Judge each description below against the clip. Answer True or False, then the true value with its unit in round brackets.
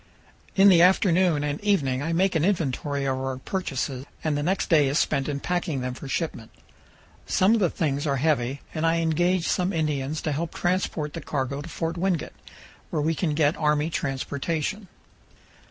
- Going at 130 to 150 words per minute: False (185 wpm)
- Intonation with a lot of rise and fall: False (3.8 semitones)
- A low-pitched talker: False (155 Hz)